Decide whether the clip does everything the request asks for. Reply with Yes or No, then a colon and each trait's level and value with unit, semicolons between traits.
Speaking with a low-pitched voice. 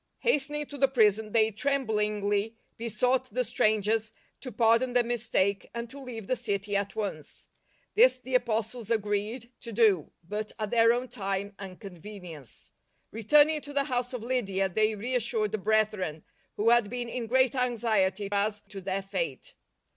No: high, 220 Hz